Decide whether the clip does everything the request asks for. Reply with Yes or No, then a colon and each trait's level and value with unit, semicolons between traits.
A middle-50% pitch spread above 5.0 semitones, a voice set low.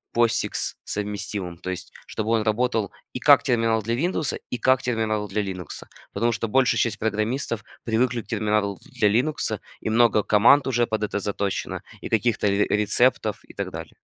No: narrow, 2.4 semitones; low, 110 Hz